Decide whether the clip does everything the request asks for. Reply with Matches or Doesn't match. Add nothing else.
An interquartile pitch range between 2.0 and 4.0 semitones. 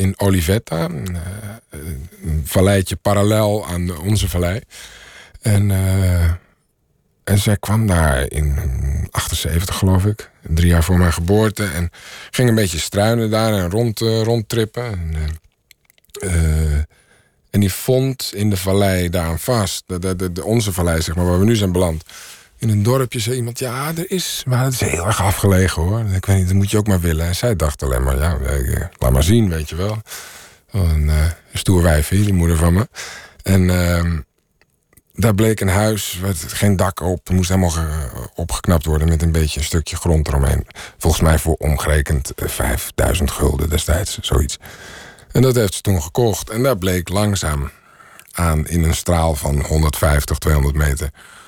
Doesn't match